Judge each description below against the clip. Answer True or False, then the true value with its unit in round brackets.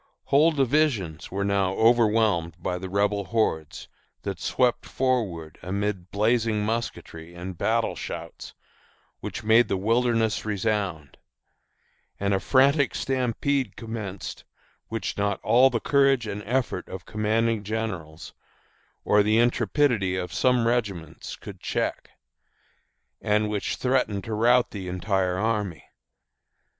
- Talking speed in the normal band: False (120 wpm)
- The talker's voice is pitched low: True (105 Hz)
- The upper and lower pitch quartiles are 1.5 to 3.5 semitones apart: False (3.9 semitones)